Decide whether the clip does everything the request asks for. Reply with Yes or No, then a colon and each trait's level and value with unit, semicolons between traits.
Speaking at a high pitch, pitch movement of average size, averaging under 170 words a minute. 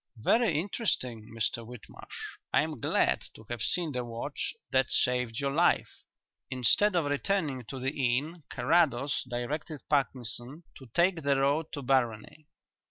No: low, 135 Hz; average, 4.4 semitones; average, 145 wpm